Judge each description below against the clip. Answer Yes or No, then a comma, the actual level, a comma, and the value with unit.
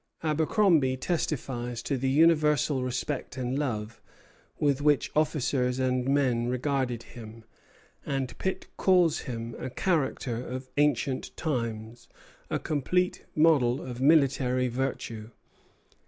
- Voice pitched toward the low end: Yes, low, 130 Hz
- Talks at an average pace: No, slow, 110 wpm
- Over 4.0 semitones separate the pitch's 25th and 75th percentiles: No, average, 3.4 semitones